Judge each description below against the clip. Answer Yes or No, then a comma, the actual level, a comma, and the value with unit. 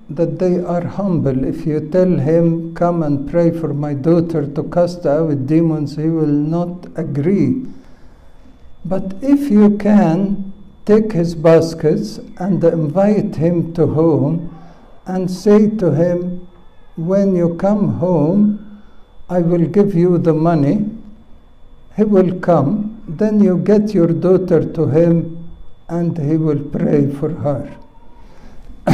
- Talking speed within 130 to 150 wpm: Yes, slow, 135 wpm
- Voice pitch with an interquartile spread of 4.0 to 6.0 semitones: No, average, 3.2 semitones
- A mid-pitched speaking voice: Yes, medium, 170 Hz